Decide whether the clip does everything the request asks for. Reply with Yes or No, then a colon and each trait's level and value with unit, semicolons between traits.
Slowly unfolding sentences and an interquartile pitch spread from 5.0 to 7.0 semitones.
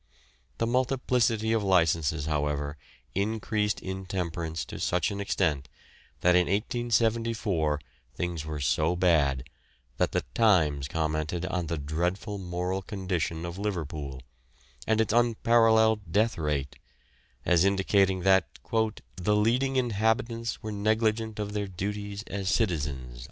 Yes: slow, 120 wpm; average, 5.3 semitones